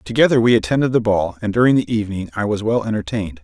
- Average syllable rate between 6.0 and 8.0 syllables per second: Yes, 7.1 syllables/s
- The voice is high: No, low, 110 Hz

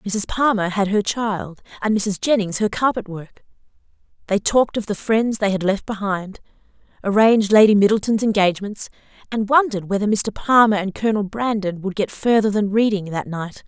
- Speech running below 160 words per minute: No, average, 170 wpm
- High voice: Yes, high, 205 Hz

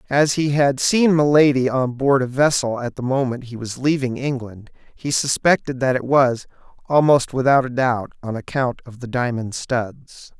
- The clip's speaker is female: No, male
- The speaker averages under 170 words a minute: No, average, 180 wpm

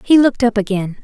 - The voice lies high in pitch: Yes, high, 225 Hz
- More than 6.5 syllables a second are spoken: Yes, 6.7 syllables/s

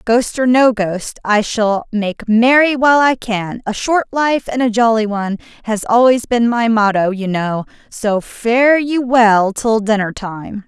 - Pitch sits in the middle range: No, high, 225 Hz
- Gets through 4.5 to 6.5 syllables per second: No, 4.1 syllables/s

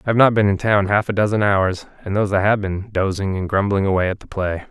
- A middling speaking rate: No, fast, 280 wpm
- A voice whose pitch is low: Yes, low, 100 Hz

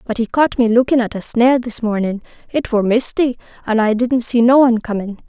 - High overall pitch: Yes, high, 235 Hz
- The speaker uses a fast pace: Yes, fast, 215 wpm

